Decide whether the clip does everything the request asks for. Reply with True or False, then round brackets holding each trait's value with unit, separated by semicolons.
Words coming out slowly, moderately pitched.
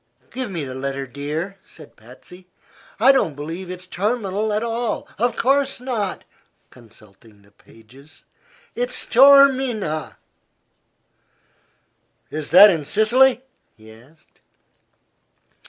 True (105 wpm; 180 Hz)